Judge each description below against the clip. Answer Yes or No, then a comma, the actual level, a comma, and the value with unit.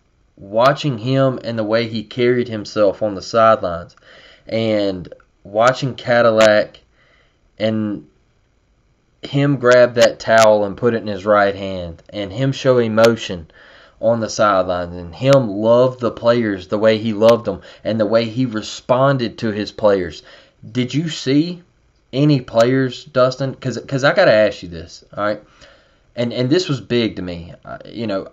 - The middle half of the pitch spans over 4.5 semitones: No, average, 3.3 semitones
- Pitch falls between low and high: No, low, 115 Hz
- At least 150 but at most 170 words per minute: Yes, average, 165 wpm